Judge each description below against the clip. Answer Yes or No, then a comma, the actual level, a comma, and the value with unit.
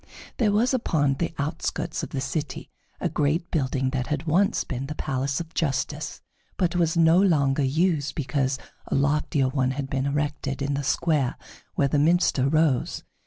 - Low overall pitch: No, medium, 145 Hz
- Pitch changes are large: No, average, 3.2 semitones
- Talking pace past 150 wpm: Yes, average, 170 wpm